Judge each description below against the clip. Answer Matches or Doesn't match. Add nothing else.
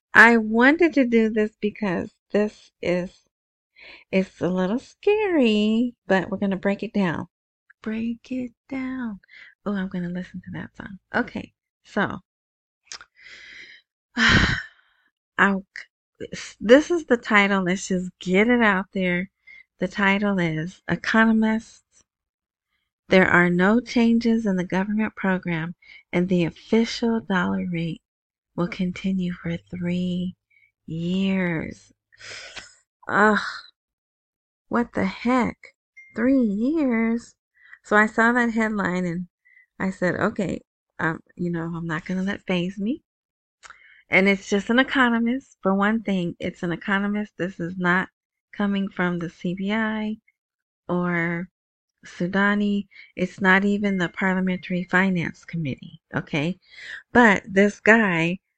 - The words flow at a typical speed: Doesn't match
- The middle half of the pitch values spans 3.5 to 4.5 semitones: Matches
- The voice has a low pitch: Doesn't match